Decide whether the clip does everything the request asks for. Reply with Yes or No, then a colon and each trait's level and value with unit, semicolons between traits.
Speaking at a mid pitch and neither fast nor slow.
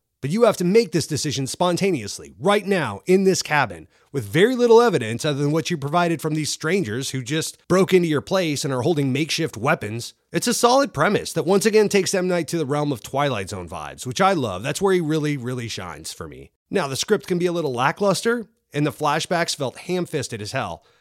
No: medium, 160 Hz; fast, 225 wpm